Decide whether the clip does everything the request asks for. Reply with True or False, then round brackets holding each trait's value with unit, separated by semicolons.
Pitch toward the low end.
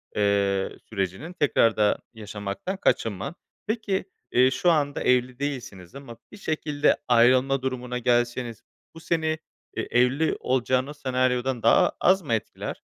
True (125 Hz)